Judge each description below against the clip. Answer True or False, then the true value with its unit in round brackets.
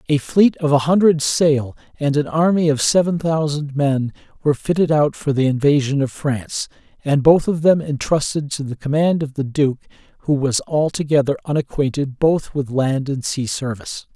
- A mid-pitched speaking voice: True (145 Hz)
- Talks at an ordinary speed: True (180 wpm)